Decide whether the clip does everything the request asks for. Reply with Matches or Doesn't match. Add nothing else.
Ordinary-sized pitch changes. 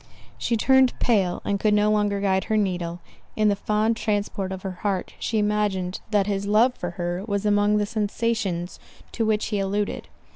Doesn't match